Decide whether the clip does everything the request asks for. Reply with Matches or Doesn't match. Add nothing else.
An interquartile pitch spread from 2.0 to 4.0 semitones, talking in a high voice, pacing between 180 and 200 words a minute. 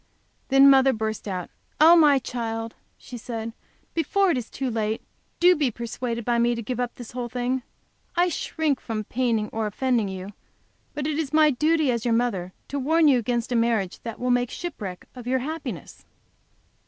Matches